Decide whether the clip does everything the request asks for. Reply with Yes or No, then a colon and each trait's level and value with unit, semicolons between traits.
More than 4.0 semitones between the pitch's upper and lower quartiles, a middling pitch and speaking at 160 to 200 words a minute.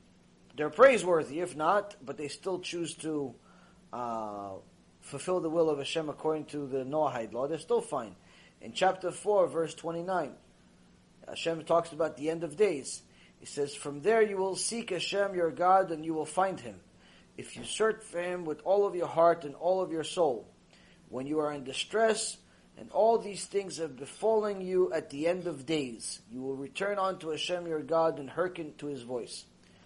Yes: average, 4.4 semitones; medium, 165 Hz; average, 190 wpm